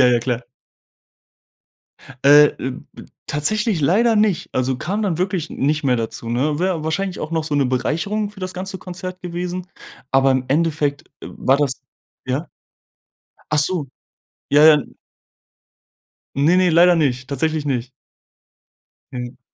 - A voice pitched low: No, medium, 155 Hz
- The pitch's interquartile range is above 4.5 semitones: Yes, average, 5.2 semitones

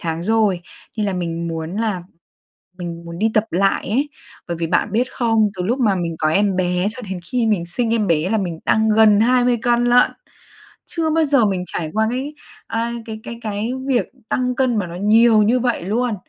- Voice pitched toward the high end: Yes, high, 215 Hz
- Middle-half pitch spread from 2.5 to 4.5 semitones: No, average, 5.0 semitones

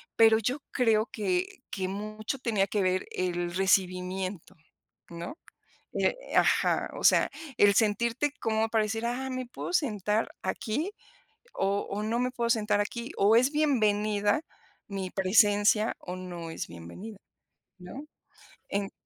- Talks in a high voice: Yes, high, 210 Hz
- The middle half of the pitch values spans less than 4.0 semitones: Yes, average, 3.5 semitones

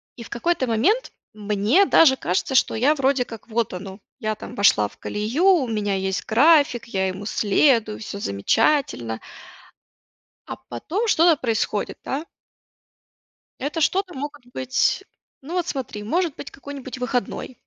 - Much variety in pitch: Yes, wide, 6.0 semitones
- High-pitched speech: Yes, high, 245 Hz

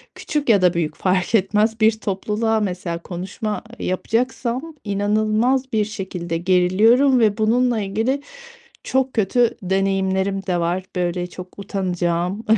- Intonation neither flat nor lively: Yes, average, 3.6 semitones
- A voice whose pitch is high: Yes, high, 200 Hz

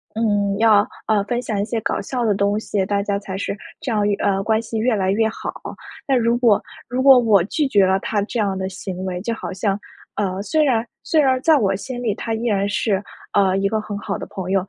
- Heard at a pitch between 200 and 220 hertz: Yes, high, 210 Hz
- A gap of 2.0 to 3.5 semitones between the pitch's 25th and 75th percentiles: Yes, average, 2.9 semitones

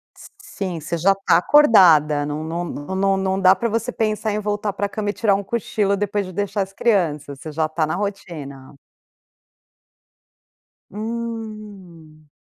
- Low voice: No, high, 195 Hz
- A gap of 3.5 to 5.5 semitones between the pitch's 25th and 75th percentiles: Yes, average, 4.3 semitones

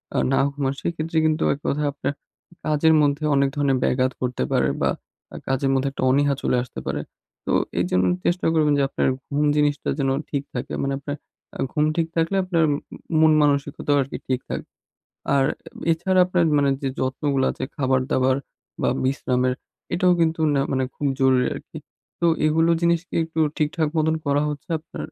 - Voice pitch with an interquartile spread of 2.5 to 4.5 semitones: Yes, average, 3.1 semitones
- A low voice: No, medium, 145 Hz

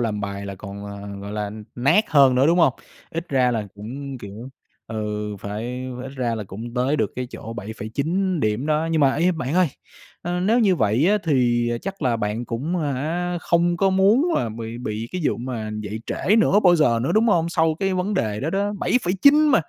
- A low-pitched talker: Yes, low, 130 Hz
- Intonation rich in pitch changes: Yes, wide, 8.0 semitones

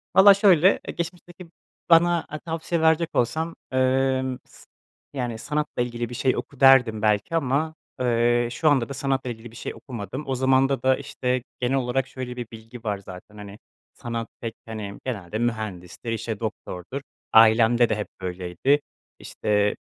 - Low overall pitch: Yes, low, 125 Hz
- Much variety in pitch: No, average, 3.7 semitones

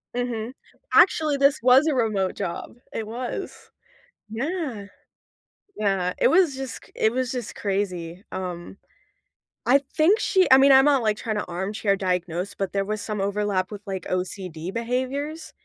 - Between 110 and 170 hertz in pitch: No, high, 215 Hz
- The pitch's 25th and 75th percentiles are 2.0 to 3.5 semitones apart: No, wide, 5.5 semitones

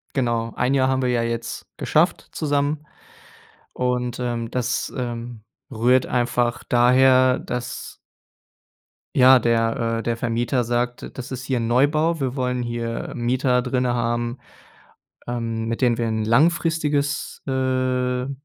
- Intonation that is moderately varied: No, narrow, 1.7 semitones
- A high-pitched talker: No, low, 125 Hz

